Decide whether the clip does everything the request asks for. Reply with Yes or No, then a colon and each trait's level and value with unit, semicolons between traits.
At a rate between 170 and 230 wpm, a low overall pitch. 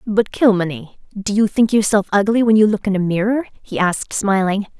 No: average, 200 wpm; high, 205 Hz